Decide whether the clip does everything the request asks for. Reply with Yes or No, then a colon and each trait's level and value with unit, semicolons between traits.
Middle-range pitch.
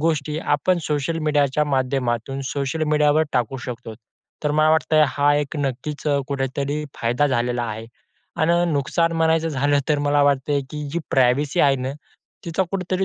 Yes: medium, 145 Hz